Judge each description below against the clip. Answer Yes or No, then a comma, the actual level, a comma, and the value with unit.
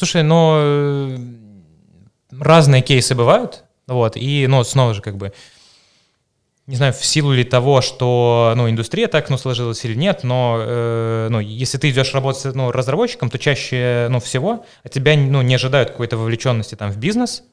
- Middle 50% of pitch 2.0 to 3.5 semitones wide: Yes, average, 3.1 semitones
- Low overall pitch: Yes, low, 130 Hz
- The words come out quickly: Yes, fast, 170 wpm